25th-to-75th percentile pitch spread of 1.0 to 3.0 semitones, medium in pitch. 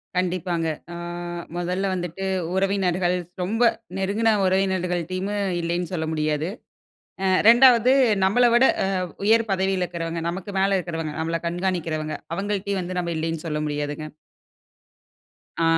Yes: average, 2.7 semitones; medium, 180 Hz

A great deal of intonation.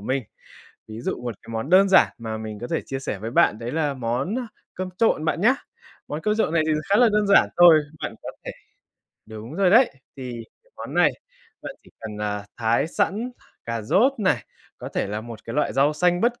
Yes: wide, 8.8 semitones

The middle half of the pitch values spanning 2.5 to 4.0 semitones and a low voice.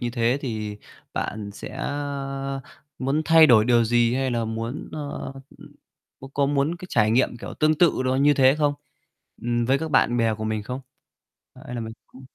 Yes: average, 3.4 semitones; low, 130 Hz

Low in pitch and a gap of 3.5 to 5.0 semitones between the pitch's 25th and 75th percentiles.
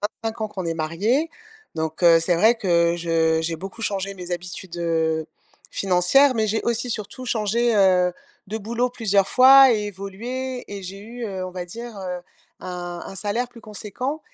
No: high, 200 Hz; average, 4.7 semitones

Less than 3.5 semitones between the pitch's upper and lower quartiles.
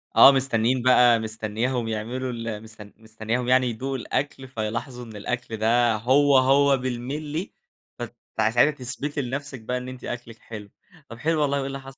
Yes: average, 3.1 semitones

